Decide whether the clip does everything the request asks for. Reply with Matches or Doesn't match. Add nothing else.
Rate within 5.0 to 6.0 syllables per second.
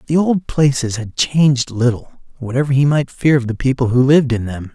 Matches